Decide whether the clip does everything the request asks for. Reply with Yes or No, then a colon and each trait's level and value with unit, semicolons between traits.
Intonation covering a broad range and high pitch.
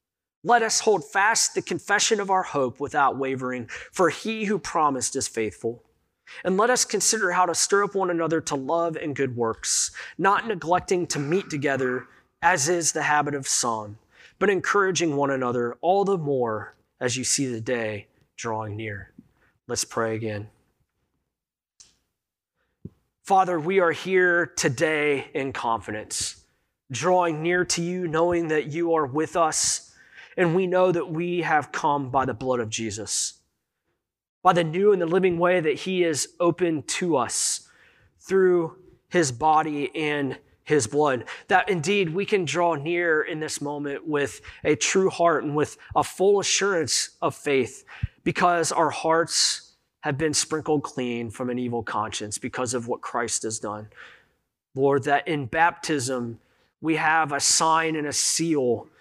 No: wide, 5.7 semitones; medium, 155 Hz